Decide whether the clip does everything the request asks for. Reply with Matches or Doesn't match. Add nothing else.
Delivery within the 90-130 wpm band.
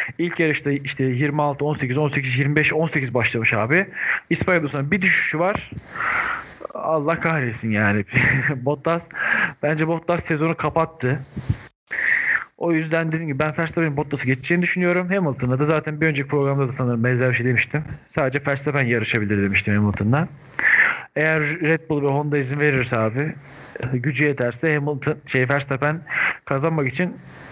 Doesn't match